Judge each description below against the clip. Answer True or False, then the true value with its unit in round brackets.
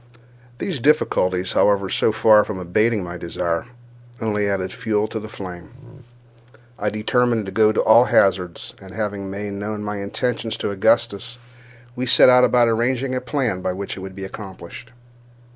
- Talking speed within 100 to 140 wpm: False (160 wpm)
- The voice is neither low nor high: False (105 Hz)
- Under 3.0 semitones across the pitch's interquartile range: False (3.4 semitones)